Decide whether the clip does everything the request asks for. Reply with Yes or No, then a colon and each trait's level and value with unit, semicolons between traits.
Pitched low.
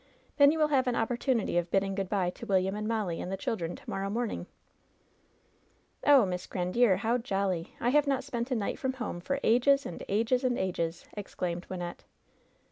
No: high, 210 Hz